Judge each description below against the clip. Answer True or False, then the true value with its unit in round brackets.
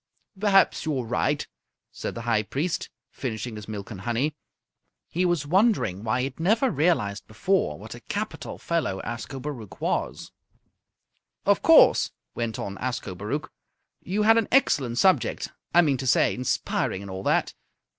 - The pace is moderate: True (150 wpm)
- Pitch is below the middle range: True (130 Hz)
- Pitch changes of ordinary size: False (8.0 semitones)